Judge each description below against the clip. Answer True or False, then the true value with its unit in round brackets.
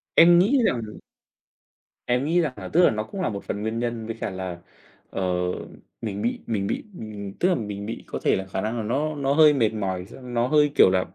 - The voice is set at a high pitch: False (115 Hz)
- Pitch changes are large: True (6.3 semitones)